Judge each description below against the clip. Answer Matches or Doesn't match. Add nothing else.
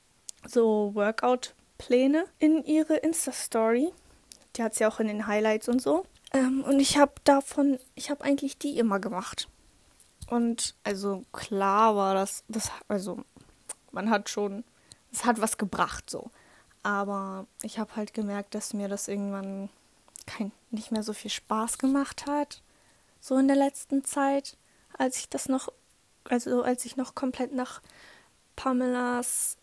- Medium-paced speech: Matches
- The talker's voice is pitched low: Doesn't match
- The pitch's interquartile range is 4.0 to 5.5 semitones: Matches